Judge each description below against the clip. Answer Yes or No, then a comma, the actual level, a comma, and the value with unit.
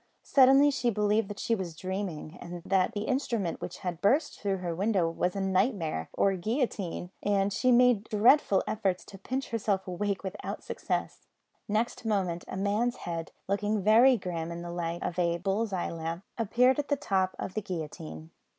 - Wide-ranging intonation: No, average, 4.2 semitones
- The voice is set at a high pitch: Yes, high, 195 Hz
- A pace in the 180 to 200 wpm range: Yes, average, 185 wpm